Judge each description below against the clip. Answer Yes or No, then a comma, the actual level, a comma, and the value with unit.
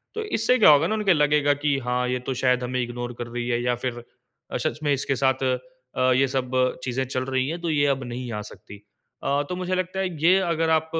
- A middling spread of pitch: Yes, average, 4.5 semitones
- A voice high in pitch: No, low, 135 Hz